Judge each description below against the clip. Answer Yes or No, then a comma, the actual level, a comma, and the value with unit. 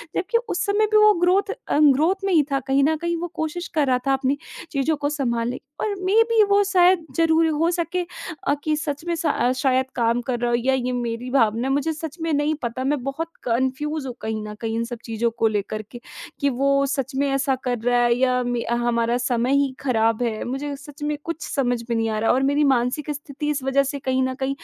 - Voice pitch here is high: Yes, very high, 275 Hz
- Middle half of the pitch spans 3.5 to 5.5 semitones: Yes, average, 4.2 semitones